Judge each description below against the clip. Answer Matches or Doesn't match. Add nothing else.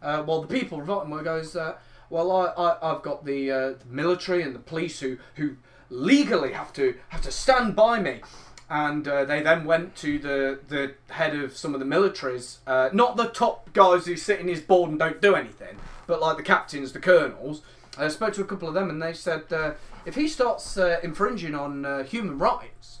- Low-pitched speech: Doesn't match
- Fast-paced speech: Matches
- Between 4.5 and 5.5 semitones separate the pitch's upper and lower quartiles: Matches